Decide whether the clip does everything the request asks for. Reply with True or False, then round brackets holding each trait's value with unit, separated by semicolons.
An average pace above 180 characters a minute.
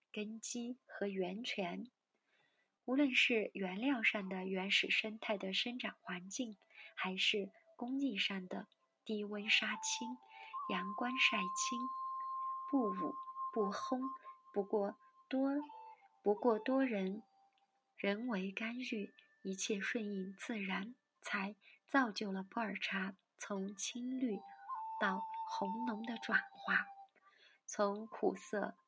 False (155 characters per minute)